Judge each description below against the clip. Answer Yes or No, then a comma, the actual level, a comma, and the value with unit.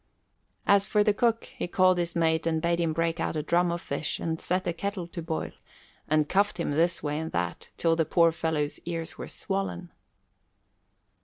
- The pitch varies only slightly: Yes, narrow, 1.9 semitones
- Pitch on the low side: No, medium, 170 Hz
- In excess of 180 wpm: Yes, average, 200 wpm